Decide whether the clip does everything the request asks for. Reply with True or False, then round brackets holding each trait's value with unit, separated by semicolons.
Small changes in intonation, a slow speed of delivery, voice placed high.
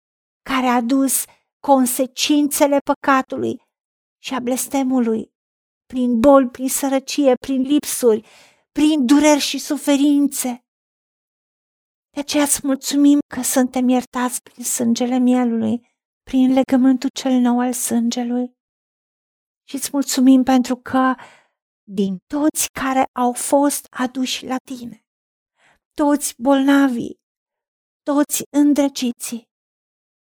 True (2.1 semitones; 100 wpm; 260 Hz)